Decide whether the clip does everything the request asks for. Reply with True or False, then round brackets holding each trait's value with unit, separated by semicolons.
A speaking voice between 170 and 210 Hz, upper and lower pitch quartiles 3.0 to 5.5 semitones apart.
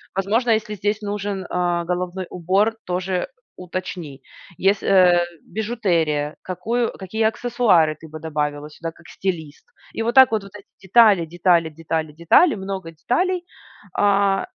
True (185 Hz; 3.9 semitones)